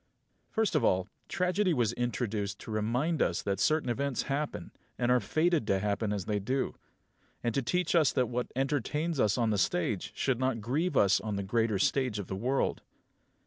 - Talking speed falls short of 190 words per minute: No, average, 195 wpm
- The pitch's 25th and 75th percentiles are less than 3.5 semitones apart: No, average, 5.3 semitones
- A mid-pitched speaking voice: No, low, 120 Hz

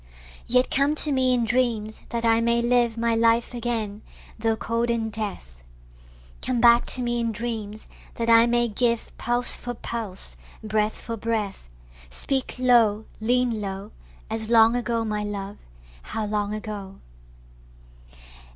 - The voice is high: Yes, high, 230 Hz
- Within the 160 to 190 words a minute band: No, average, 145 wpm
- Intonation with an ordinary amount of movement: No, narrow, 1.9 semitones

